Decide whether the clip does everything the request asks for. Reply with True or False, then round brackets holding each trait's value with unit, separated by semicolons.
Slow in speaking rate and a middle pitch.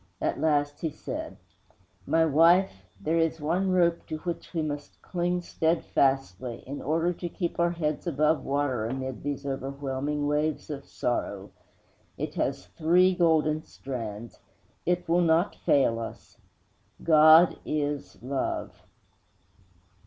True (130 wpm; 150 Hz)